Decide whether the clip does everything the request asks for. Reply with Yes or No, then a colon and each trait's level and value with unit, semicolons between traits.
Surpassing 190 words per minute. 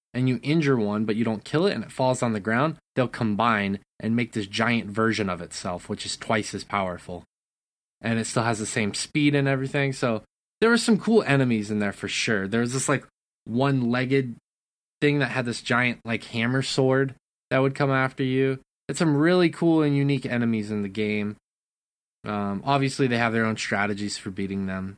Yes: fast, 205 wpm